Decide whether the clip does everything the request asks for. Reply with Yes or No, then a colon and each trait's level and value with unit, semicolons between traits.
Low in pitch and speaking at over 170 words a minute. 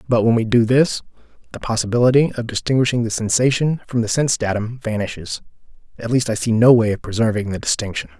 Yes: low, 115 Hz; average, 190 wpm